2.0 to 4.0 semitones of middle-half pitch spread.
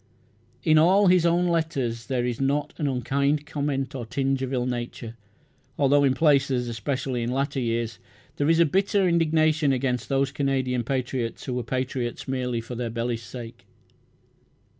Yes: average, 3.1 semitones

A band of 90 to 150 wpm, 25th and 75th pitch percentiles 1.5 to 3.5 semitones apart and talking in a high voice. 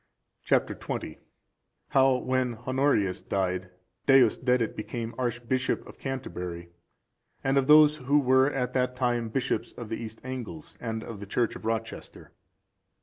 No: average, 140 wpm; average, 2.9 semitones; low, 125 Hz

